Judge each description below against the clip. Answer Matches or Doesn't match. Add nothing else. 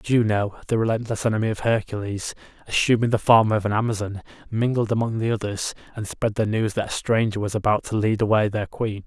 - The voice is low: Matches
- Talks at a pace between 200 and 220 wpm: Matches